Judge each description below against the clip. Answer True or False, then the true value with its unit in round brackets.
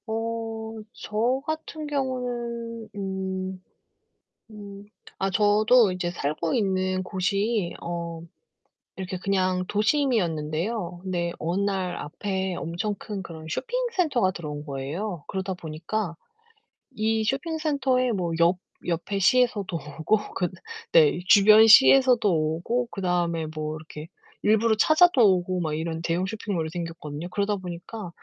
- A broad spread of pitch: False (4.6 semitones)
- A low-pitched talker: False (195 Hz)